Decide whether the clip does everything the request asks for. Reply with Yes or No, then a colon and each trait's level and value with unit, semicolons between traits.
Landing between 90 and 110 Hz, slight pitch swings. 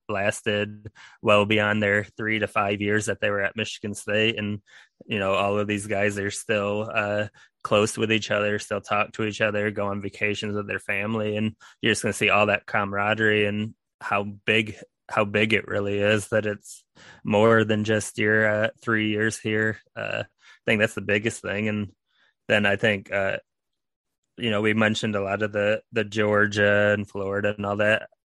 Yes: low, 105 Hz; narrow, 1.0 semitones